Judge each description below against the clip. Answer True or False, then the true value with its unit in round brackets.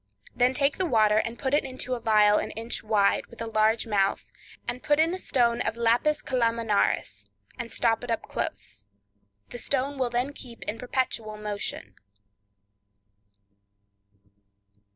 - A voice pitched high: True (230 Hz)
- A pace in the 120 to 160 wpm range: True (150 wpm)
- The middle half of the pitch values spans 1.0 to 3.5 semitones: True (3.1 semitones)